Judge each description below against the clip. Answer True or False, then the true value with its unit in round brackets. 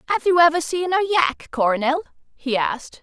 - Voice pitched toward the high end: True (305 Hz)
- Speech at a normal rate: True (180 wpm)